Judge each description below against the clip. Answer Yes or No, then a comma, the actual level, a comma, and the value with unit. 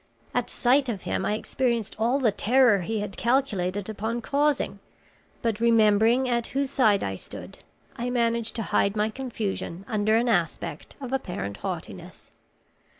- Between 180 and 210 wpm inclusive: No, average, 150 wpm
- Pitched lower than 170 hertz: No, high, 225 Hz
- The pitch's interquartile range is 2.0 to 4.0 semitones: Yes, average, 3.2 semitones